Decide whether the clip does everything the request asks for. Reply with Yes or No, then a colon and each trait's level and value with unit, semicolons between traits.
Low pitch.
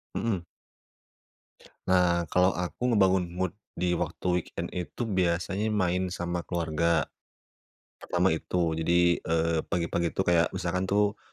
Yes: very low, 90 Hz